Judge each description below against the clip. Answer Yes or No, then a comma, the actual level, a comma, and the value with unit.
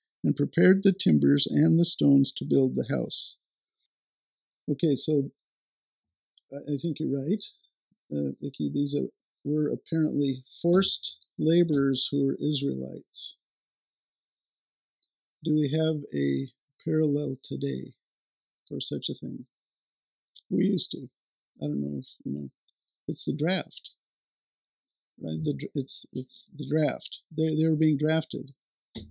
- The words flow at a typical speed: No, slow, 125 wpm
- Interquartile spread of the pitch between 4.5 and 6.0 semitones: No, average, 3.6 semitones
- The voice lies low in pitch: No, medium, 145 Hz